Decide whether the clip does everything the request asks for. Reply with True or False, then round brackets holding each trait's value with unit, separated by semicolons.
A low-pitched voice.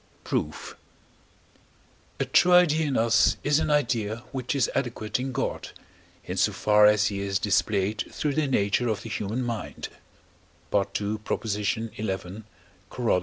True (110 Hz)